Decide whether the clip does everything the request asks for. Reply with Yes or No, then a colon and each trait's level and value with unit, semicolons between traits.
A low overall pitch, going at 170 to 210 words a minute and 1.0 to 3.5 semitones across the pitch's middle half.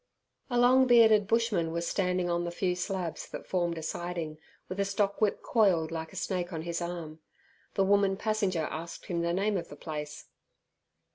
No: medium, 180 Hz; average, 185 wpm; average, 3.1 semitones